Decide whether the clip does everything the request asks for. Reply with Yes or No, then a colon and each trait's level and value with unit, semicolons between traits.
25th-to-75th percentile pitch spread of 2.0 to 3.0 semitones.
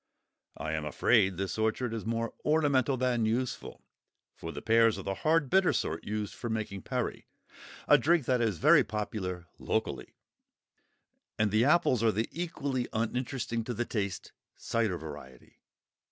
No: average, 4.2 semitones